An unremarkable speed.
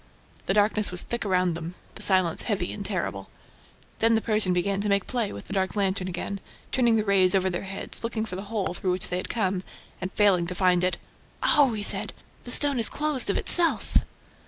No: fast, 215 wpm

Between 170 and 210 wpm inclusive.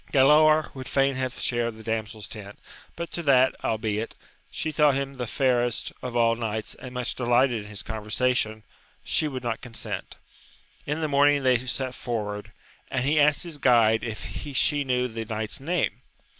Yes: average, 175 wpm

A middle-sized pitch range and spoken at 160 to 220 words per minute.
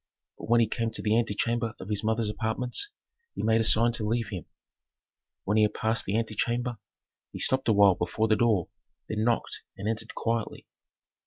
No: narrow, 1.6 semitones; average, 190 wpm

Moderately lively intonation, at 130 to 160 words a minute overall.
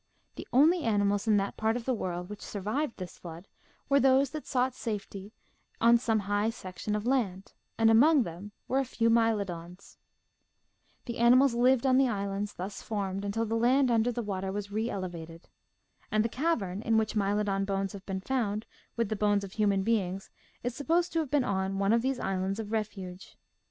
No: average, 3.5 semitones; average, 190 wpm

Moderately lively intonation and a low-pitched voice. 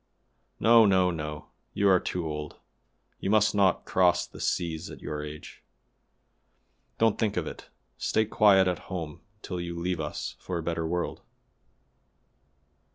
Yes: average, 3.3 semitones; very low, 90 Hz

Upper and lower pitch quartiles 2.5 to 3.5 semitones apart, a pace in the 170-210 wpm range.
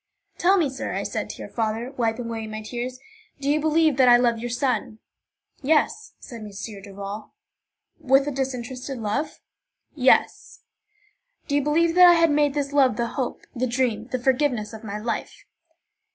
No: average, 4.0 semitones; average, 175 wpm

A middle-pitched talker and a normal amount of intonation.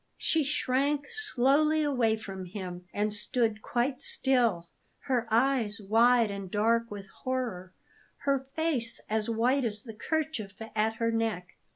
No: high, 230 Hz; average, 4.2 semitones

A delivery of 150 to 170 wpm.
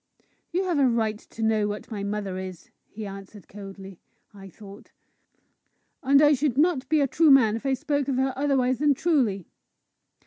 No: average, 180 wpm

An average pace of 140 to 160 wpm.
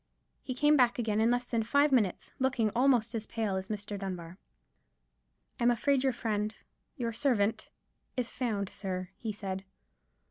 Yes: average, 145 wpm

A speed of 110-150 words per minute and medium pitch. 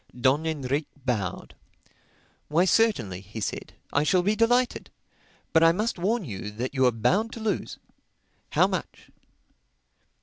Yes: average, 140 wpm; medium, 155 Hz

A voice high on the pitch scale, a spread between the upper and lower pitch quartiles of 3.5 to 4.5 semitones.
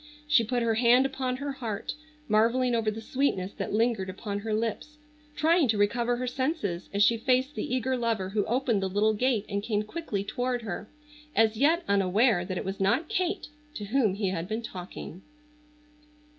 Yes: high, 225 Hz; average, 4.0 semitones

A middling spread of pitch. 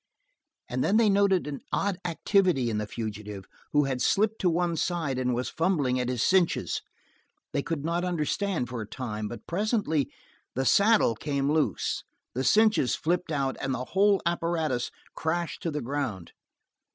No: wide, 6.1 semitones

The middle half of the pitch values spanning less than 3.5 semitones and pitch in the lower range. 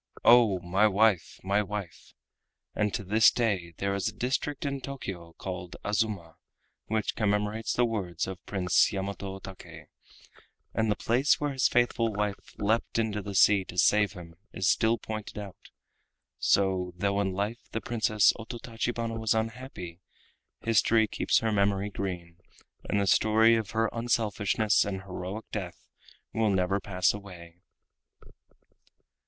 Yes: average, 2.7 semitones; low, 105 Hz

